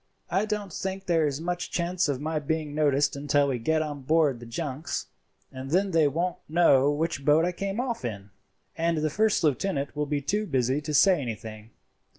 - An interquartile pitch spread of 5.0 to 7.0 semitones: No, average, 4.0 semitones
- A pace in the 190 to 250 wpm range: Yes, average, 195 wpm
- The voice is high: No, medium, 155 Hz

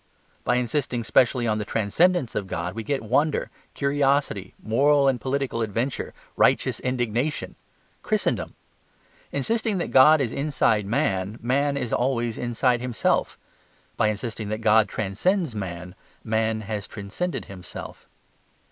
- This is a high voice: No, low, 120 Hz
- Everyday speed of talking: No, slow, 130 wpm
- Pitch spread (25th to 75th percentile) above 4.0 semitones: Yes, average, 4.5 semitones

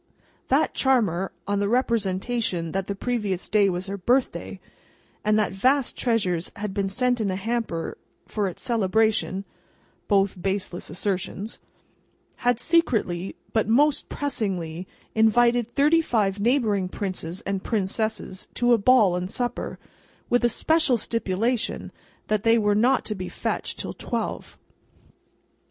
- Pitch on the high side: Yes, high, 210 Hz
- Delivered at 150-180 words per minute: No, slow, 135 wpm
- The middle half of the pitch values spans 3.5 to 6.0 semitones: Yes, average, 3.9 semitones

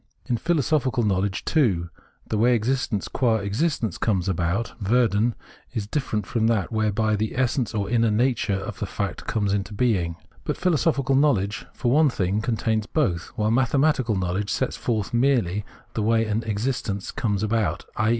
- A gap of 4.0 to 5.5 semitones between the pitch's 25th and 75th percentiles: No, average, 3.6 semitones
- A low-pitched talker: Yes, low, 110 Hz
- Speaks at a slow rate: No, average, 160 wpm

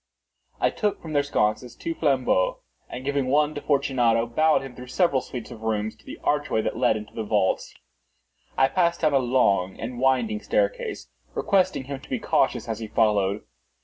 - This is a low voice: Yes, low, 130 Hz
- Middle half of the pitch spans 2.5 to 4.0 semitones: No, average, 5.2 semitones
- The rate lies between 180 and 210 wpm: Yes, average, 185 wpm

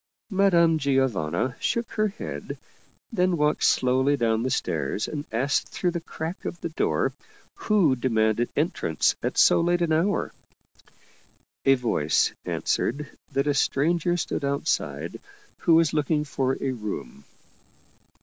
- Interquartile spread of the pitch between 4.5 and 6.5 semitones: Yes, average, 5.1 semitones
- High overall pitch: No, medium, 145 Hz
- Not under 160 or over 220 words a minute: No, slow, 135 wpm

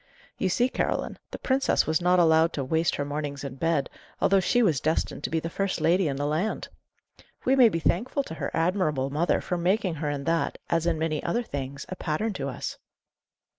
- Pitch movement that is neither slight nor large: Yes, average, 4.0 semitones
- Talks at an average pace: No, fast, 210 wpm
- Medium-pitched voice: Yes, medium, 165 Hz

